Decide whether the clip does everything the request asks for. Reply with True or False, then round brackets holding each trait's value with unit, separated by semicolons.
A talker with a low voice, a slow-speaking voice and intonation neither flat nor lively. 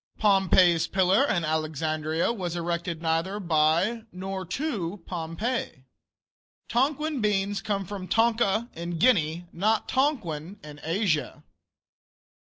False (185 Hz; 105 wpm; 4.6 semitones)